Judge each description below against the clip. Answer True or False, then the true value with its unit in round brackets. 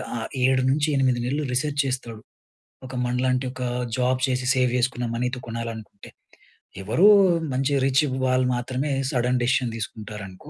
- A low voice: True (125 Hz)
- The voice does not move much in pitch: True (1.6 semitones)